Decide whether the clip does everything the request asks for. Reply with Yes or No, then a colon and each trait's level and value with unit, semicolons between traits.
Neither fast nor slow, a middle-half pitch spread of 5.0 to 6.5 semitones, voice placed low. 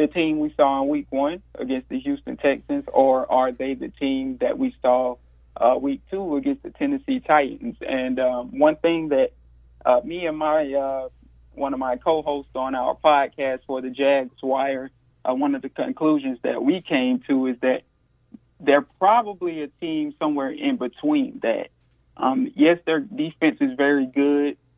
No: average, 175 wpm; wide, 5.5 semitones; medium, 145 Hz